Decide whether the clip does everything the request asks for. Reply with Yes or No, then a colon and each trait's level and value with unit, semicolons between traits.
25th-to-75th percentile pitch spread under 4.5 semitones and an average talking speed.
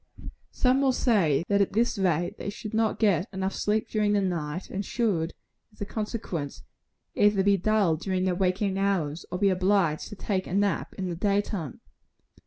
Yes: average, 2.7 semitones; average, 190 wpm